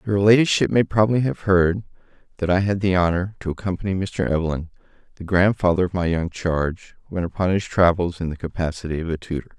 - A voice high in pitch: No, very low, 90 Hz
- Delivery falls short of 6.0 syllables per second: No, 6.2 syllables/s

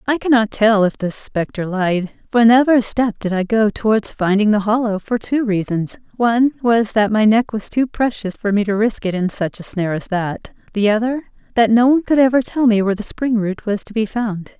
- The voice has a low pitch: No, high, 220 Hz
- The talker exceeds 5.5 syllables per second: No, 5.3 syllables/s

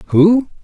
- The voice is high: Yes, high, 200 Hz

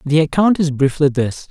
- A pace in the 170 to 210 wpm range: Yes, average, 200 wpm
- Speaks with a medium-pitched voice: Yes, medium, 150 Hz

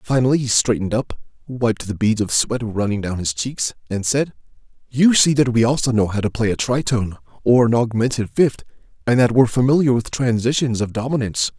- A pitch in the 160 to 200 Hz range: No, low, 120 Hz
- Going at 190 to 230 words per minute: Yes, average, 195 wpm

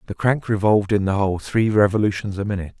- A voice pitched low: Yes, low, 100 Hz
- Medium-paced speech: No, fast, 215 wpm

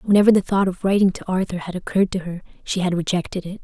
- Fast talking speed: Yes, fast, 250 wpm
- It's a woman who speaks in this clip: Yes, female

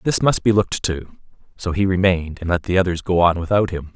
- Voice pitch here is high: No, very low, 90 Hz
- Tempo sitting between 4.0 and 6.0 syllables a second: No, 6.2 syllables/s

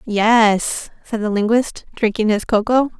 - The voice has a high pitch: Yes, high, 220 Hz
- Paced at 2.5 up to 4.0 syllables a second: Yes, 3.9 syllables/s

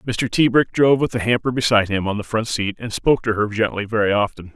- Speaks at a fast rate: Yes, fast, 250 wpm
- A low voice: Yes, low, 110 Hz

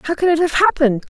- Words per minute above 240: Yes, fast, 260 wpm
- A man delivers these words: No, female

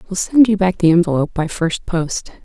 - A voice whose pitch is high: No, medium, 180 Hz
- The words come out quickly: Yes, fast, 220 wpm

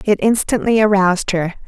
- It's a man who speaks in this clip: No, female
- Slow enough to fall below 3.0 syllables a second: No, 5.4 syllables/s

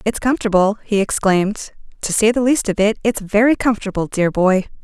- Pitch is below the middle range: No, high, 210 Hz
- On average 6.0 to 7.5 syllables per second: No, 5.7 syllables/s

